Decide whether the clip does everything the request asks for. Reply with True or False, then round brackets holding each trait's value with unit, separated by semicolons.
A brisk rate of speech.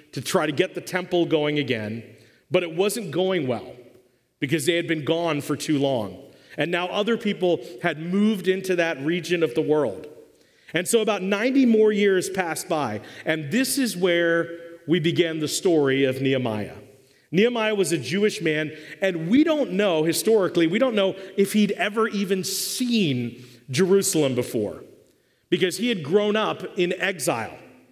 False (170 wpm)